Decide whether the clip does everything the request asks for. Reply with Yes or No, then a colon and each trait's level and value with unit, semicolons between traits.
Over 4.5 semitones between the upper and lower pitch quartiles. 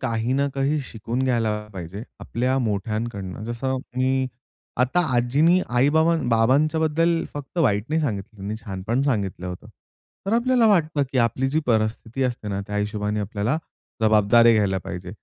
Yes: average, 5.0 semitones